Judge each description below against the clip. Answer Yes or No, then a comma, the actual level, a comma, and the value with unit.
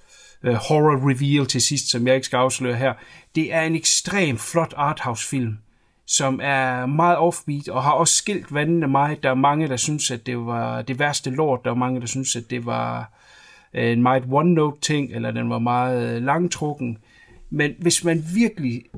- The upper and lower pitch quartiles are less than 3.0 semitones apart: No, average, 3.7 semitones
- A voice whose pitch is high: No, low, 135 Hz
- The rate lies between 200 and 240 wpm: No, average, 185 wpm